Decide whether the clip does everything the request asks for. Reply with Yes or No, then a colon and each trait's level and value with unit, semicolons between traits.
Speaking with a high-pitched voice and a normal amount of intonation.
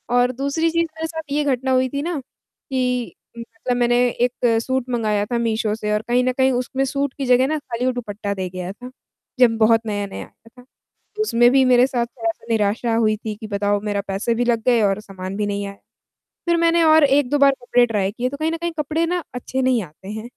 Yes: high, 245 Hz; average, 3.8 semitones